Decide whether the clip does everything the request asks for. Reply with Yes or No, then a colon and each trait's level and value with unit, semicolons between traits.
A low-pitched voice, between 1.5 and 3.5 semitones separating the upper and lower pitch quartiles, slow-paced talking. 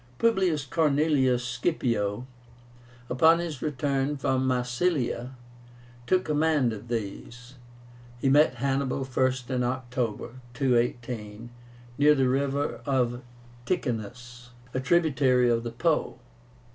Yes: low, 130 Hz; average, 3.1 semitones; slow, 100 wpm